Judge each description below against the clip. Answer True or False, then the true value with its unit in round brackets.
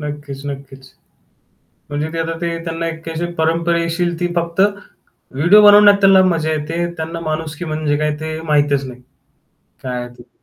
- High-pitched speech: False (160 Hz)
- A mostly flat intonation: True (2.3 semitones)